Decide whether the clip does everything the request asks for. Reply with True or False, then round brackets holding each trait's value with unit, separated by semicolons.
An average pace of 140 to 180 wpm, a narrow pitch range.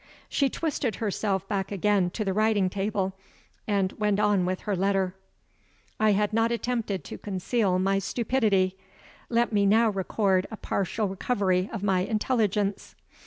True (150 wpm; 2.2 semitones)